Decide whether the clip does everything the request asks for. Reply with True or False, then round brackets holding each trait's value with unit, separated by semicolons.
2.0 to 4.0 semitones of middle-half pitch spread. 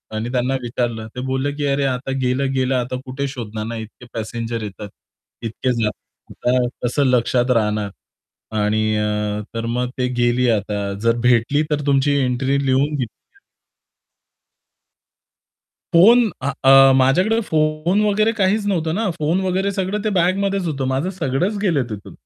False (5.4 semitones)